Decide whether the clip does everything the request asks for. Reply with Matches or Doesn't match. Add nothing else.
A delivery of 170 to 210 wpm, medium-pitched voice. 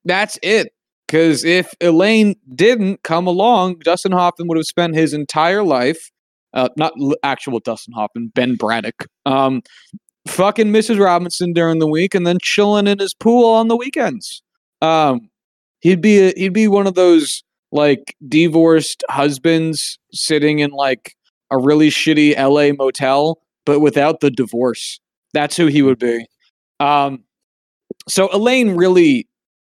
Doesn't match